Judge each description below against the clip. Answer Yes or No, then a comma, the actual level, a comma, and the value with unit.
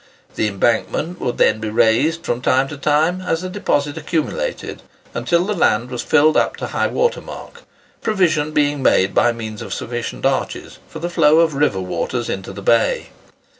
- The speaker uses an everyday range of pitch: No, wide, 6.1 semitones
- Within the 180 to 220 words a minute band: Yes, average, 185 wpm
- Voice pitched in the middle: Yes, medium, 145 Hz